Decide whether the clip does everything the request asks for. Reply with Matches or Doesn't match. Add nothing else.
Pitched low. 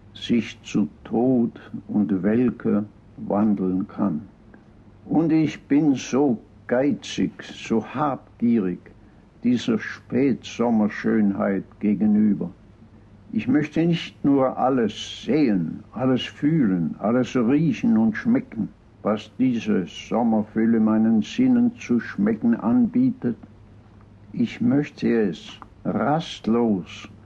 Matches